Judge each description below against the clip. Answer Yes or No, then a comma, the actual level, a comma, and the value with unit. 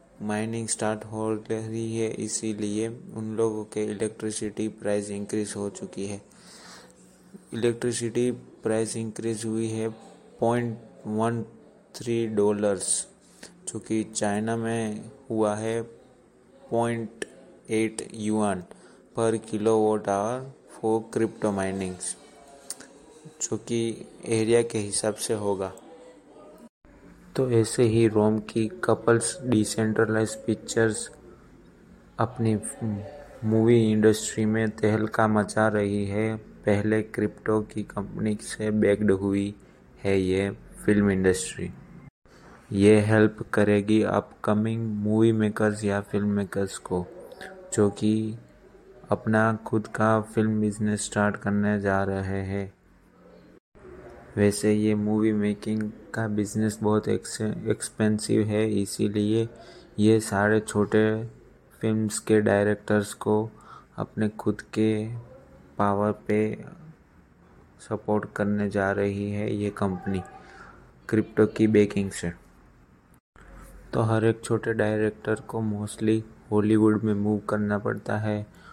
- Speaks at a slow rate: Yes, slow, 105 wpm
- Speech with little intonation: Yes, narrow, 1.3 semitones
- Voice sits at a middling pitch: No, low, 110 Hz